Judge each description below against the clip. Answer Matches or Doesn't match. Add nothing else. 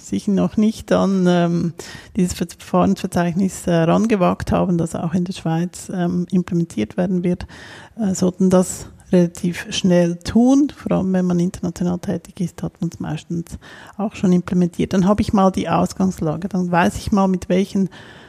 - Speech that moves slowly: Doesn't match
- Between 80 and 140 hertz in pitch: Doesn't match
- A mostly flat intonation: Matches